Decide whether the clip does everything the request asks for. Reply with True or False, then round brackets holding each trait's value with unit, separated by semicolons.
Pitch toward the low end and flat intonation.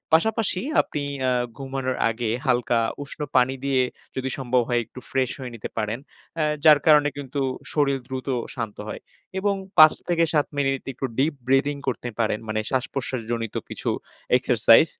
False (130 Hz; 3.1 semitones)